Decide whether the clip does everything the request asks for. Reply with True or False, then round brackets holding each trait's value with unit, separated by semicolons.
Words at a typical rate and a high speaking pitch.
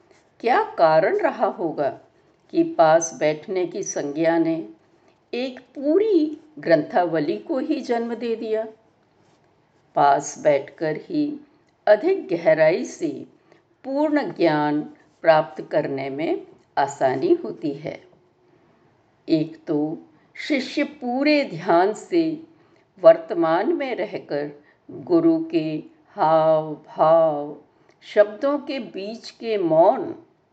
False (100 wpm; 275 Hz)